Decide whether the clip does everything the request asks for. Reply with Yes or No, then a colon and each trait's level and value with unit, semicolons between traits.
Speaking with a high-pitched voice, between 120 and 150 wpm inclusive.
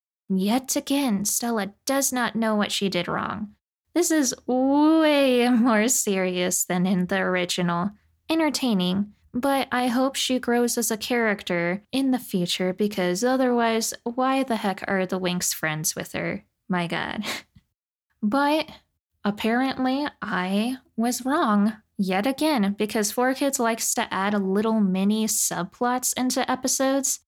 Yes: high, 225 Hz; average, 140 wpm